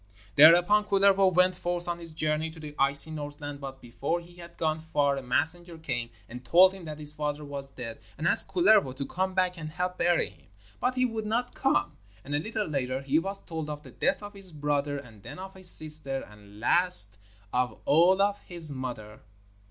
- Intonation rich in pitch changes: No, average, 4.6 semitones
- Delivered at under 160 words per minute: No, fast, 205 wpm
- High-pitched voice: No, medium, 155 Hz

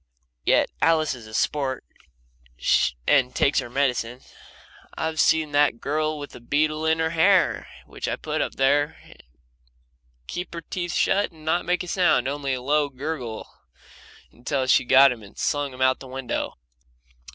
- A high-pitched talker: No, medium, 145 Hz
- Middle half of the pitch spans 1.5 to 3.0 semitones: No, average, 3.5 semitones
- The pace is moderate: Yes, average, 165 wpm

